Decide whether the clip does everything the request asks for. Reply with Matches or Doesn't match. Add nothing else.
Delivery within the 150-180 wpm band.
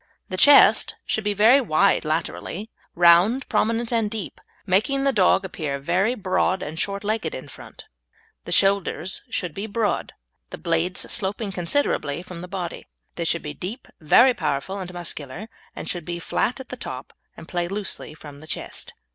Matches